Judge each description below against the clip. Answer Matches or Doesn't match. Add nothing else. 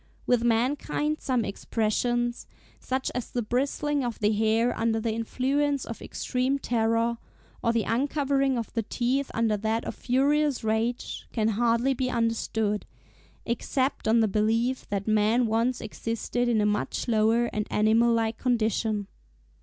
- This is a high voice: Matches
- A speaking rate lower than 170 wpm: Matches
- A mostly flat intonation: Matches